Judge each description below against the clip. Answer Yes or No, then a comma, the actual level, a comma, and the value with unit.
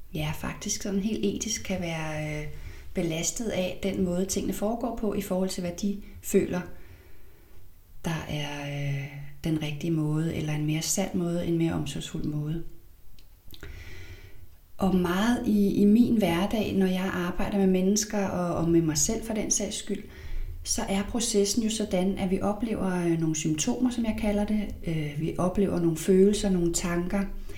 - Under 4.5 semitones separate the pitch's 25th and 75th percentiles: No, average, 4.9 semitones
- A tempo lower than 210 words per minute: Yes, average, 165 wpm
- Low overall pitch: No, medium, 180 Hz